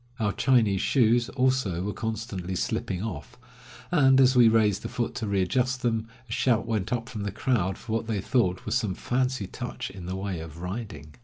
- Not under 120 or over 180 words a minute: No, average, 200 wpm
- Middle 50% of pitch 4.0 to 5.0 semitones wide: Yes, average, 4.4 semitones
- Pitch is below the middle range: Yes, low, 110 Hz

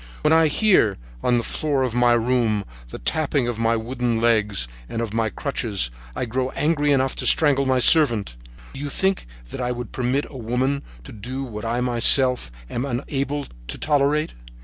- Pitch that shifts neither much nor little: Yes, average, 3.4 semitones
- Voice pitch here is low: Yes, low, 125 Hz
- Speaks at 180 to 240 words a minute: Yes, average, 185 wpm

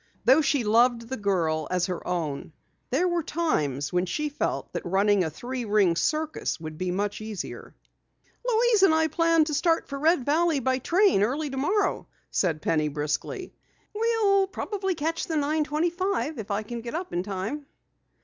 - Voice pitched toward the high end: Yes, very high, 270 Hz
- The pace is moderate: Yes, average, 170 wpm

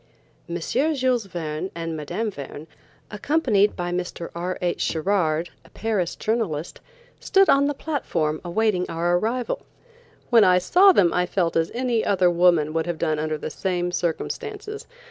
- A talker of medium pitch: Yes, medium, 180 Hz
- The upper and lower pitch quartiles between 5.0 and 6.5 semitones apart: Yes, wide, 5.4 semitones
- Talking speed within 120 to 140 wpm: No, average, 155 wpm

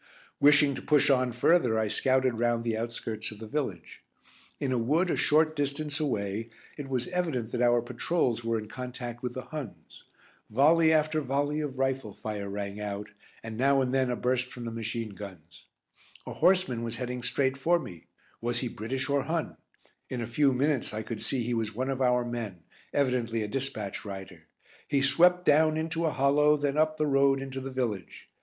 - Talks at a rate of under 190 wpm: No, average, 195 wpm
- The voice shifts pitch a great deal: No, average, 4.0 semitones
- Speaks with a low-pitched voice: Yes, low, 130 Hz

